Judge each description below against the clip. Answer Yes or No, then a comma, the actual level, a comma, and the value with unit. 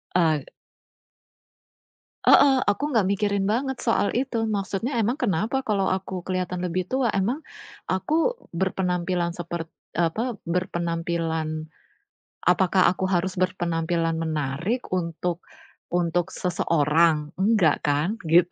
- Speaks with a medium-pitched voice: Yes, medium, 180 Hz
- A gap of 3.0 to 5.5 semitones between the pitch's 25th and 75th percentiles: Yes, average, 3.6 semitones